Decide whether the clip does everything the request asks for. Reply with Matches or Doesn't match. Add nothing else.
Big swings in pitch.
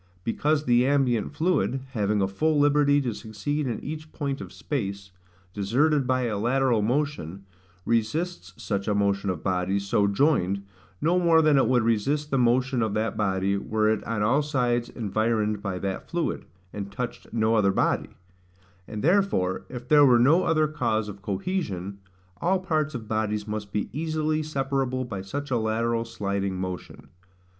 Matches